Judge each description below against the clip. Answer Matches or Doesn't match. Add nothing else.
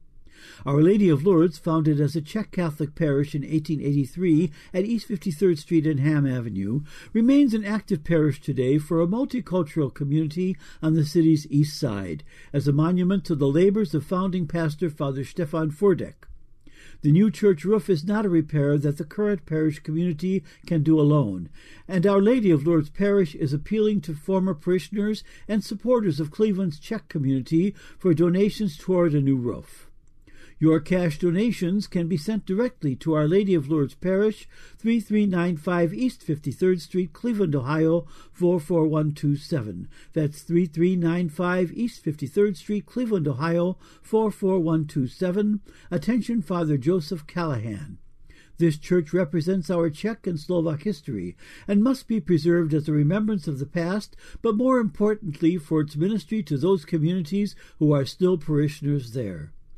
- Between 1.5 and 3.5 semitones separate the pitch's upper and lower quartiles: Doesn't match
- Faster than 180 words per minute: Doesn't match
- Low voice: Doesn't match